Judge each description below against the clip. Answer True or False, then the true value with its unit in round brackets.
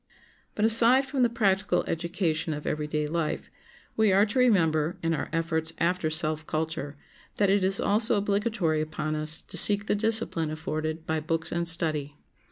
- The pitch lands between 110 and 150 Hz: False (165 Hz)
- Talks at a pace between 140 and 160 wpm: False (170 wpm)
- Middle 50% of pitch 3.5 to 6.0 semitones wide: True (4.6 semitones)